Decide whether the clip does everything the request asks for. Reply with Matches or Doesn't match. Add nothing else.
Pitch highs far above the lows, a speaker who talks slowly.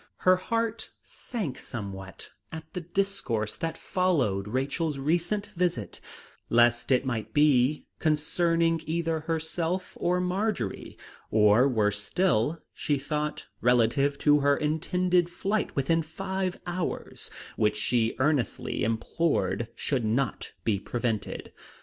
Matches